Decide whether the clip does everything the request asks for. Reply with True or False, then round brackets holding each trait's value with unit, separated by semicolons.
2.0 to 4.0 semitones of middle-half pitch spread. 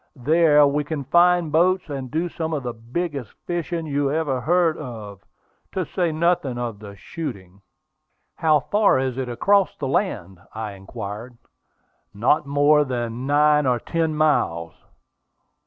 False (5.1 semitones)